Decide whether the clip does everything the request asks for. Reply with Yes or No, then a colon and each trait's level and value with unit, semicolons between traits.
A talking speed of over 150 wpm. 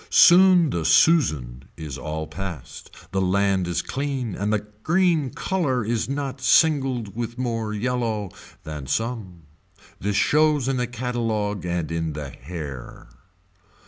No: slow, 135 wpm